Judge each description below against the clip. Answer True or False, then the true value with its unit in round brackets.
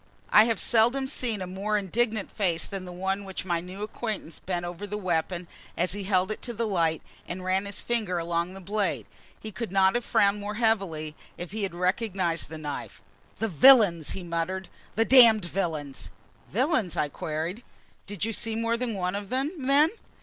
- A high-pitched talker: True (195 Hz)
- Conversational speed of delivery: True (195 wpm)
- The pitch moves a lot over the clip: False (4.0 semitones)